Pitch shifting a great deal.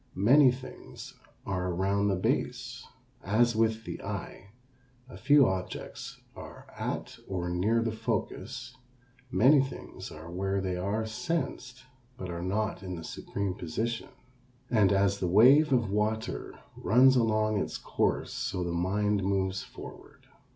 No: average, 3.8 semitones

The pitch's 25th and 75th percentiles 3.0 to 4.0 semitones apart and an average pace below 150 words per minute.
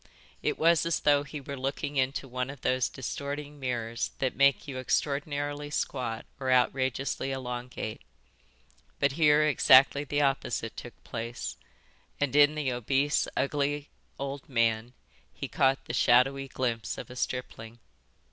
No: narrow, 2.4 semitones; average, 140 wpm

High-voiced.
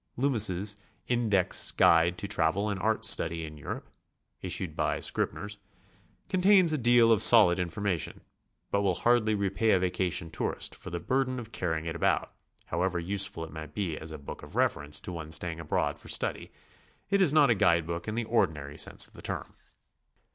No: very low, 95 Hz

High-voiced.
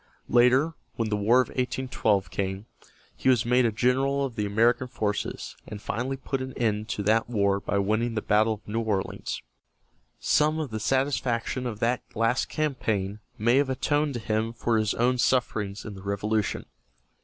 No: low, 115 Hz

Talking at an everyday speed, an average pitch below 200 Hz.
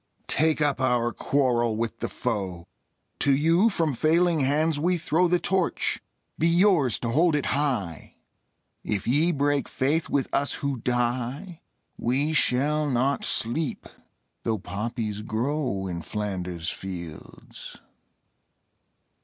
No: slow, 125 wpm; low, 135 Hz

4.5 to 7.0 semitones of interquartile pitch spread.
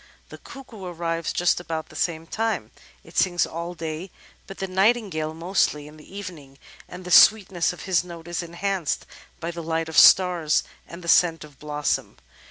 No: narrow, 2.4 semitones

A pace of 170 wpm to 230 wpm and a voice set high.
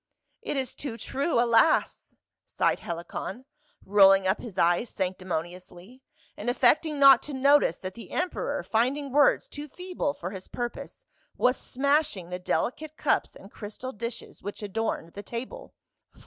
No: average, 150 wpm; high, 235 Hz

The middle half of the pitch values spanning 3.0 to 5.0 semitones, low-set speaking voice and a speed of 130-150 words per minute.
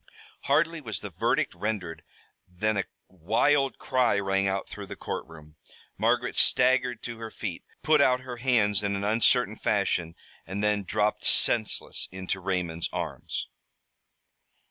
Yes: average, 4.4 semitones; low, 105 Hz; average, 140 wpm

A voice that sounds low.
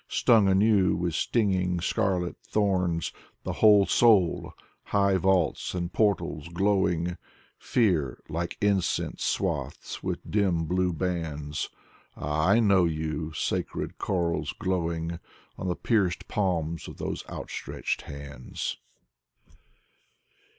Yes: very low, 90 Hz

